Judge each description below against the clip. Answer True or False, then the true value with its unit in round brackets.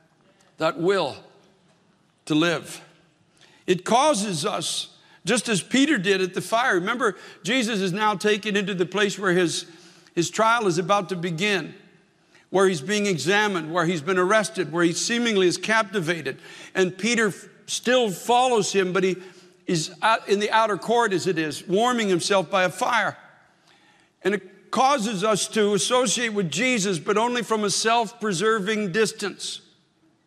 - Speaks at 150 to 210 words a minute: True (155 wpm)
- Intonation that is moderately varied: True (3.4 semitones)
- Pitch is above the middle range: True (195 Hz)